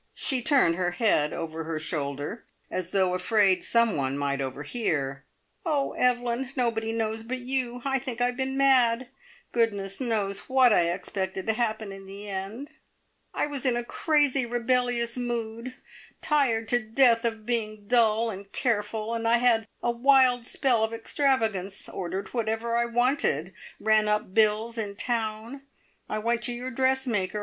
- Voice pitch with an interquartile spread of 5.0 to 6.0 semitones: No, average, 3.6 semitones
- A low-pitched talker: No, high, 230 Hz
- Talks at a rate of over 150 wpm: Yes, average, 160 wpm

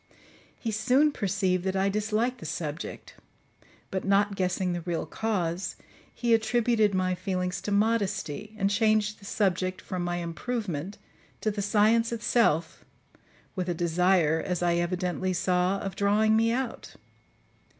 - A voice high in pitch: Yes, high, 195 Hz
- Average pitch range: Yes, average, 3.3 semitones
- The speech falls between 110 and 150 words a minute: Yes, average, 140 wpm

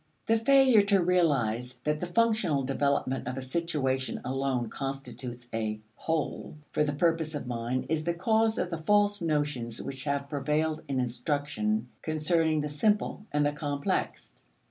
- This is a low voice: No, medium, 145 Hz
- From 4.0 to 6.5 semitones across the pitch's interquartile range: Yes, average, 4.4 semitones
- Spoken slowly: No, average, 155 wpm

